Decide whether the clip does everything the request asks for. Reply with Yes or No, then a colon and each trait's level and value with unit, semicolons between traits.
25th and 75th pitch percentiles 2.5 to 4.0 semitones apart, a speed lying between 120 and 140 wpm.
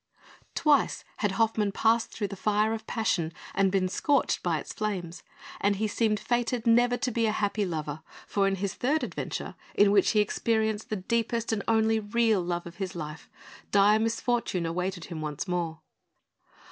No: average, 3.4 semitones; average, 175 wpm